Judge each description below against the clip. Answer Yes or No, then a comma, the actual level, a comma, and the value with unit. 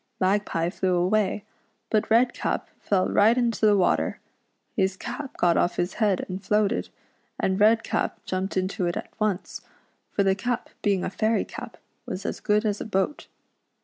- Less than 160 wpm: No, average, 170 wpm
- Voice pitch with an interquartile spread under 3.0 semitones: Yes, narrow, 2.4 semitones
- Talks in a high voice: Yes, high, 200 Hz